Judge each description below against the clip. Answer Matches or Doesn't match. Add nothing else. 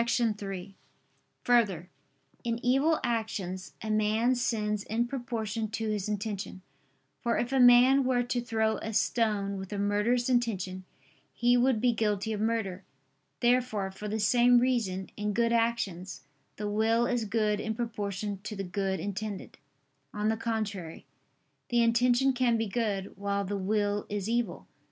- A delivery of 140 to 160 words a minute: Matches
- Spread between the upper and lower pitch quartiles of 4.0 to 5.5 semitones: Doesn't match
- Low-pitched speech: Doesn't match